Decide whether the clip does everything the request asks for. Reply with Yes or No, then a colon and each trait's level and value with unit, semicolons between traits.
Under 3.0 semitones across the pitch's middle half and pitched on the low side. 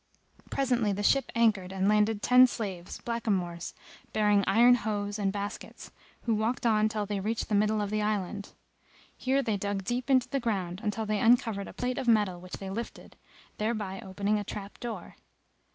No: narrow, 2.6 semitones; high, 210 Hz